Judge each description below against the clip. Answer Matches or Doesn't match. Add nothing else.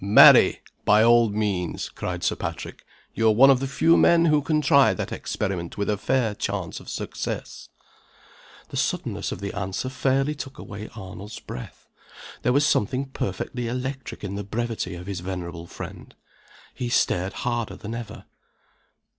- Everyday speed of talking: Matches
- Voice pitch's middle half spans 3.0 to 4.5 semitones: Doesn't match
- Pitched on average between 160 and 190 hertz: Doesn't match